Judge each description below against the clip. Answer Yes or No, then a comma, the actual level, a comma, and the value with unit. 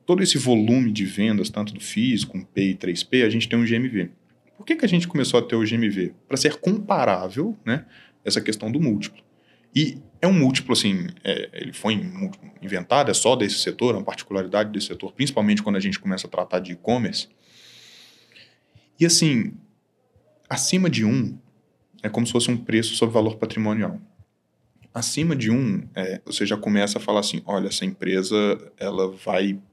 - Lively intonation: Yes, wide, 8.1 semitones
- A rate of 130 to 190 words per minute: Yes, fast, 185 wpm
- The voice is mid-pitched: No, low, 115 Hz